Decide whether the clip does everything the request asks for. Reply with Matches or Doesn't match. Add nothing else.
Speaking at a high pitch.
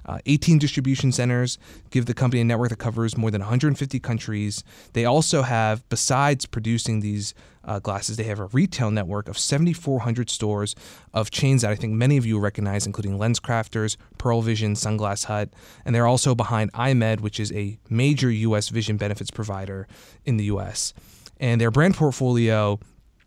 Doesn't match